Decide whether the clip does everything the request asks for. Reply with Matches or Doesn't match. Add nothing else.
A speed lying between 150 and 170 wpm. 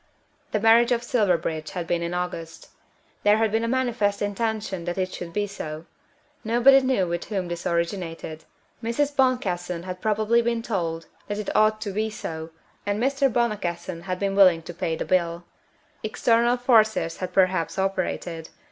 Matches